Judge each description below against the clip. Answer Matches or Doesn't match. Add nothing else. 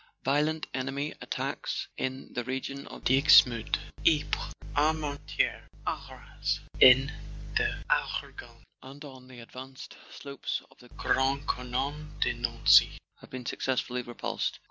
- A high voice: Doesn't match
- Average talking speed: Doesn't match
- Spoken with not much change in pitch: Matches